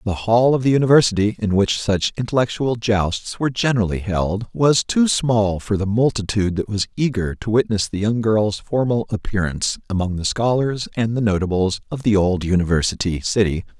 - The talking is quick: No, average, 175 wpm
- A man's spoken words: Yes, male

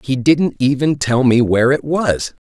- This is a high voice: No, low, 135 Hz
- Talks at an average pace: Yes, average, 195 wpm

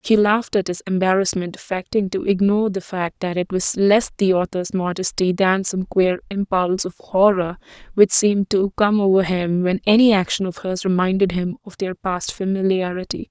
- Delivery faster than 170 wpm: Yes, average, 180 wpm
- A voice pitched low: No, high, 190 Hz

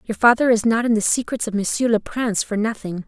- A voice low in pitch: No, high, 220 Hz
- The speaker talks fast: Yes, fast, 255 wpm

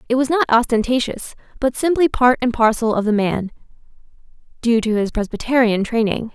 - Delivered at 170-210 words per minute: No, average, 160 wpm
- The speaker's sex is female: Yes, female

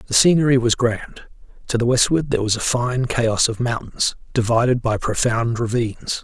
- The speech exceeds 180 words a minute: No, average, 175 wpm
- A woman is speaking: No, male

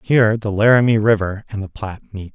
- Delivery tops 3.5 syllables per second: Yes, 5.9 syllables/s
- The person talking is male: Yes, male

